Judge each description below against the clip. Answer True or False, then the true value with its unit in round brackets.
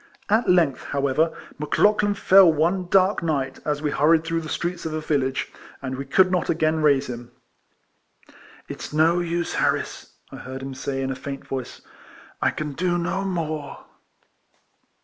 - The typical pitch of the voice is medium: True (155 Hz)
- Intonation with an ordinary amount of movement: True (4.1 semitones)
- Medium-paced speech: True (175 wpm)